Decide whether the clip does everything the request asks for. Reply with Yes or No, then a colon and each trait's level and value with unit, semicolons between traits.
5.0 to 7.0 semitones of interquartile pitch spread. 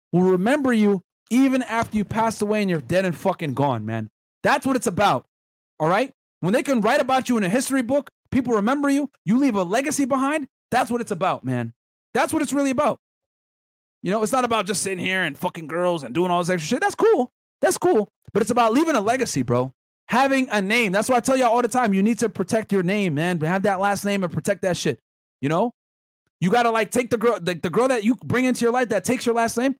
Yes: wide, 5.6 semitones